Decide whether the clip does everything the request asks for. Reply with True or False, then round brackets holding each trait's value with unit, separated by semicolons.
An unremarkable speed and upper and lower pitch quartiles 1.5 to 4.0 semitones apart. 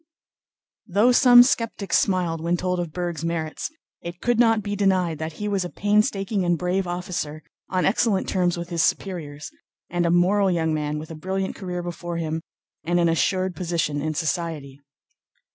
True (175 wpm; 2.8 semitones)